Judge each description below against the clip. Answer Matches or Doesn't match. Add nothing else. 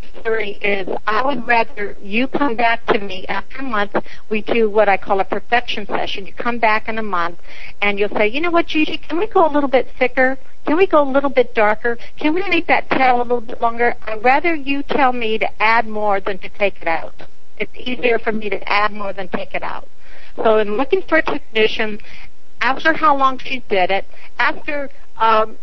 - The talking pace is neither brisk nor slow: Doesn't match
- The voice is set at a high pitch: Matches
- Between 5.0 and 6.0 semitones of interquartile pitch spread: Doesn't match